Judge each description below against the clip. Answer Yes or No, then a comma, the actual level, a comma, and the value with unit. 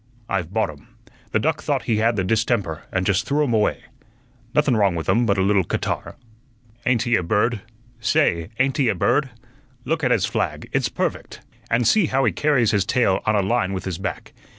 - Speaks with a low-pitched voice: Yes, low, 110 Hz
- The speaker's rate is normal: No, fast, 210 wpm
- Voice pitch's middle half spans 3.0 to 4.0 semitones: No, average, 4.4 semitones